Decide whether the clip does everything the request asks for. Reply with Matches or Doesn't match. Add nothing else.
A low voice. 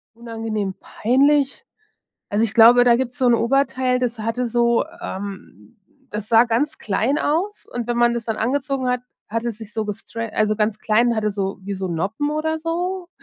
Doesn't match